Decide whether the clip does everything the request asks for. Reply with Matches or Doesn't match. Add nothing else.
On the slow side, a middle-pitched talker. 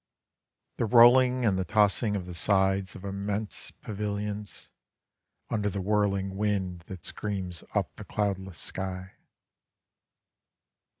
Doesn't match